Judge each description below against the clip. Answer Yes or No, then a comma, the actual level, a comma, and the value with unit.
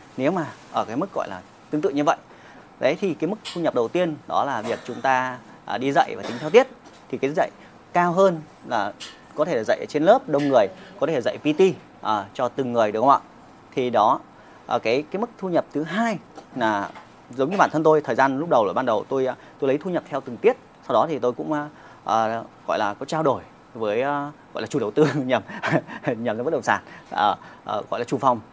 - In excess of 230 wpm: Yes, average, 240 wpm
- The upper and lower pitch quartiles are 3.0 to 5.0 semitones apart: No, wide, 5.4 semitones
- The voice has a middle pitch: Yes, medium, 145 Hz